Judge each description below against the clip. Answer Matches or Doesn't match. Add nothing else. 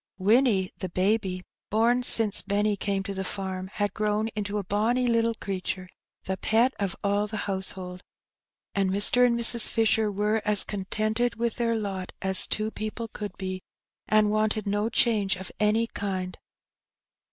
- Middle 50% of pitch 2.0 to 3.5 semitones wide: Matches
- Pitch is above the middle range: Matches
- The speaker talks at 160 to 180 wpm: Matches